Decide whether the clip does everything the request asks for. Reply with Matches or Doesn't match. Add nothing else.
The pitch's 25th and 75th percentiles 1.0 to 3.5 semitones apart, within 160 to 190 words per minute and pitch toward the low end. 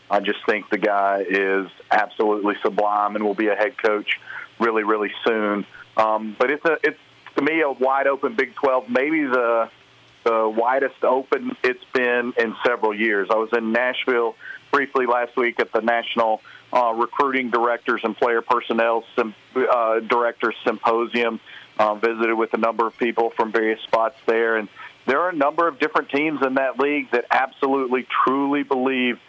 Matches